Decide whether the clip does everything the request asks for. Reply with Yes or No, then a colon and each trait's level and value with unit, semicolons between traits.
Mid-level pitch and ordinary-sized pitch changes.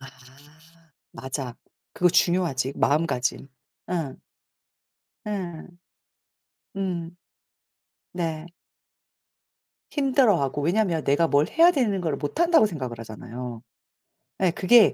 No: medium, 165 Hz; wide, 6.1 semitones